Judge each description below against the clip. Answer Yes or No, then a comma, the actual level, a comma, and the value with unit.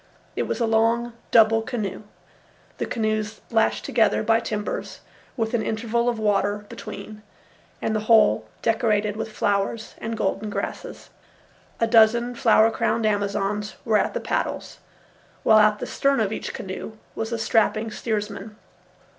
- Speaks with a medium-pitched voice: No, high, 220 Hz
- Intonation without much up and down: Yes, narrow, 1.5 semitones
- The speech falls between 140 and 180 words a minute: Yes, average, 145 wpm